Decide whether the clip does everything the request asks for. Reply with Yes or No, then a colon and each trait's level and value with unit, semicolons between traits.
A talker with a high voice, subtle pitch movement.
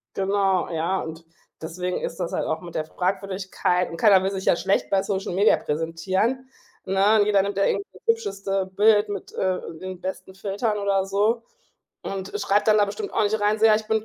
Yes: high, 195 Hz; narrow, 1.9 semitones